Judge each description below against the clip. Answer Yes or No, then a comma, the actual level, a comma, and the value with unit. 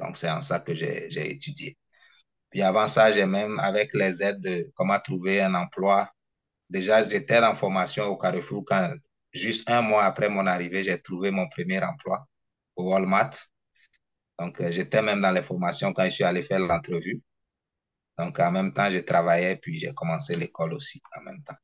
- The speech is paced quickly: No, average, 190 wpm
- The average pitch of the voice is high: No, low, 100 Hz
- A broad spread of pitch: No, average, 2.7 semitones